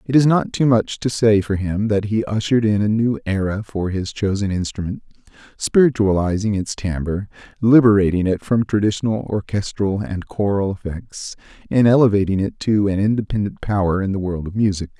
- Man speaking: Yes, male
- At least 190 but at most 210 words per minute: No, average, 170 wpm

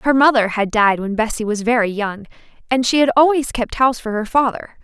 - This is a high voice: Yes, high, 235 Hz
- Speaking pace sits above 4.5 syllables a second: Yes, 5.5 syllables/s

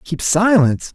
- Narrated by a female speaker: No, male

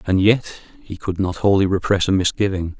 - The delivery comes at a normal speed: Yes, average, 195 wpm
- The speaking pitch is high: No, very low, 95 Hz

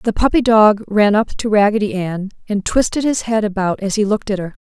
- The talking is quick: Yes, fast, 235 wpm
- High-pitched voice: Yes, high, 210 Hz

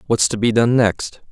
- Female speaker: No, male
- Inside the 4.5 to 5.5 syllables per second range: Yes, 4.6 syllables/s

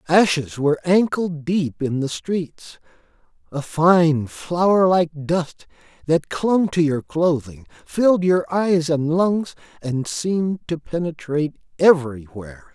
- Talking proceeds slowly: Yes, slow, 120 wpm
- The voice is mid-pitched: Yes, medium, 160 Hz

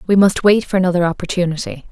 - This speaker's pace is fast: No, average, 190 wpm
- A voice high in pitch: No, medium, 180 Hz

